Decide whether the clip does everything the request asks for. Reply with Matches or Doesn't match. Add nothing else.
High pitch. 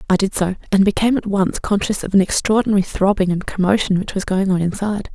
Matches